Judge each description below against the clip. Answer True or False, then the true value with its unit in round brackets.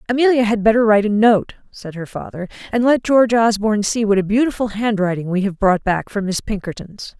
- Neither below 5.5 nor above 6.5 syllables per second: True (5.9 syllables/s)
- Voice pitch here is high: True (215 Hz)